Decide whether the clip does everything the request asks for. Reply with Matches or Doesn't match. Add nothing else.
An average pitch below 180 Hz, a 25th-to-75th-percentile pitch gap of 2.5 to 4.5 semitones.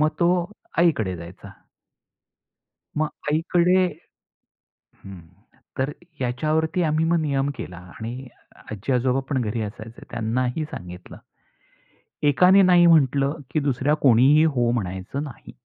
Doesn't match